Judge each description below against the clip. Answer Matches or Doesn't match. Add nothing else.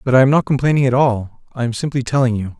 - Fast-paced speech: Matches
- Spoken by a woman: Doesn't match